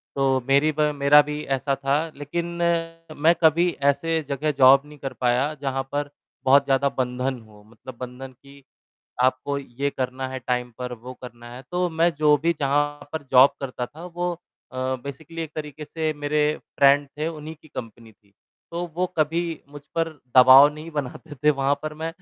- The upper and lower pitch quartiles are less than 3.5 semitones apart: Yes, average, 2.9 semitones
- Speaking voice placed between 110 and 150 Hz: Yes, medium, 140 Hz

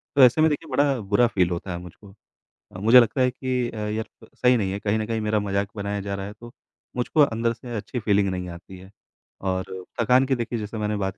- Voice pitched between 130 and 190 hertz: No, low, 110 Hz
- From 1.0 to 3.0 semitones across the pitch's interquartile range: No, average, 3.8 semitones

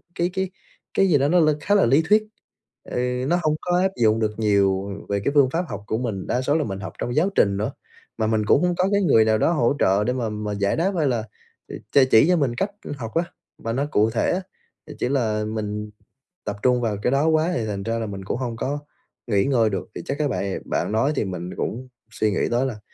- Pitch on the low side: Yes, low, 120 Hz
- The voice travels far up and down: Yes, wide, 5.8 semitones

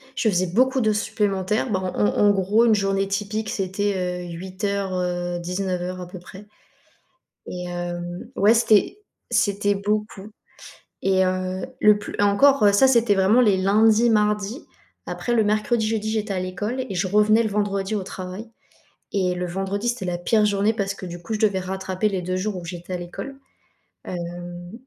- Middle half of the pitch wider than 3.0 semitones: No, average, 2.7 semitones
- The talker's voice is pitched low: No, high, 195 Hz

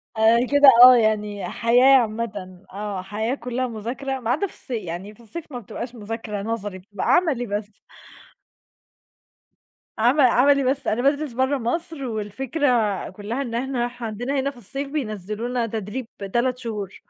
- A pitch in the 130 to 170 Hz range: No, high, 235 Hz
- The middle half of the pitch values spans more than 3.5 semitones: Yes, average, 3.9 semitones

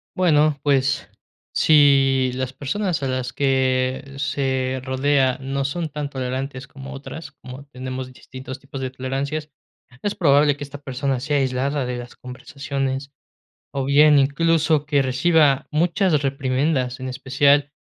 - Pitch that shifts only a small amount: Yes, narrow, 1.8 semitones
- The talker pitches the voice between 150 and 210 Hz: No, low, 135 Hz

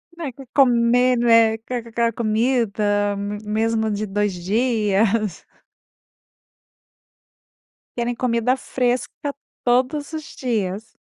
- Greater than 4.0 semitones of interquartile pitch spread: No, average, 3.0 semitones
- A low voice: No, high, 230 Hz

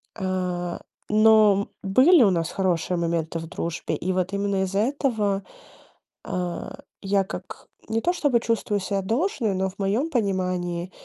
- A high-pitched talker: Yes, high, 195 Hz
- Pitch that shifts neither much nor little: Yes, average, 3.3 semitones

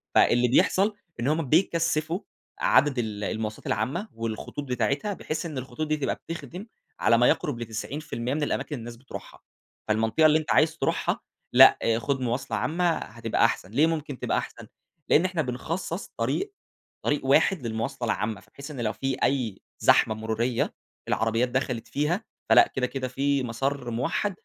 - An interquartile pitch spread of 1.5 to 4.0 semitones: No, average, 5.0 semitones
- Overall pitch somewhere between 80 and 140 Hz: Yes, low, 135 Hz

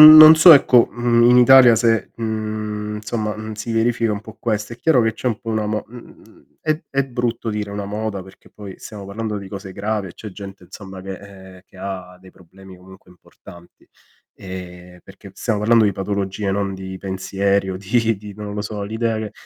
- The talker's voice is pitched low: Yes, low, 105 Hz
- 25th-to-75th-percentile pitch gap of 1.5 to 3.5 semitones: Yes, average, 2.7 semitones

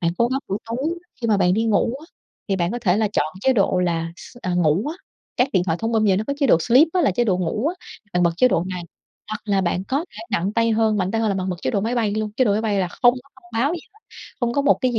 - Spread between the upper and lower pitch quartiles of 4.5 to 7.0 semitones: Yes, average, 4.8 semitones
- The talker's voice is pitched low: No, high, 215 Hz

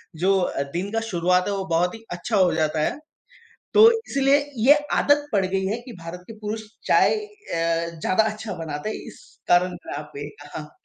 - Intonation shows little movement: No, average, 5.0 semitones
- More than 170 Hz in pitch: Yes, high, 190 Hz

